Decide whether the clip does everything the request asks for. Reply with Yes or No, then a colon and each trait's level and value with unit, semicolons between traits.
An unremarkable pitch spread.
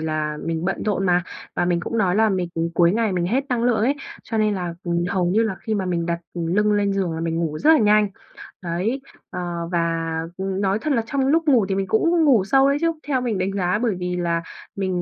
Yes: average, 4.3 semitones